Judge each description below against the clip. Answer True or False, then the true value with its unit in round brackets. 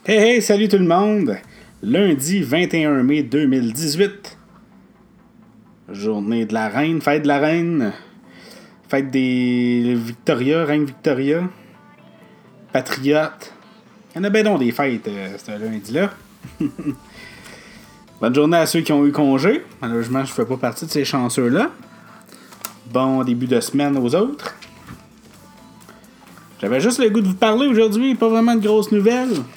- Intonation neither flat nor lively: False (8.3 semitones)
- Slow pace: True (140 wpm)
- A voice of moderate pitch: True (150 Hz)